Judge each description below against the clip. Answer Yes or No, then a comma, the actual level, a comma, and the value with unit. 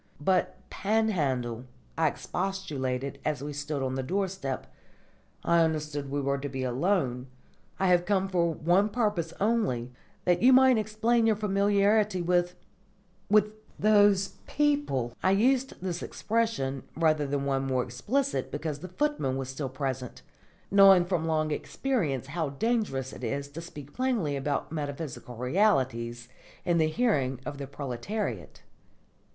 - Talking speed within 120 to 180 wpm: Yes, average, 140 wpm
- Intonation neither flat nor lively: No, wide, 7.0 semitones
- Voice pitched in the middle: Yes, medium, 160 Hz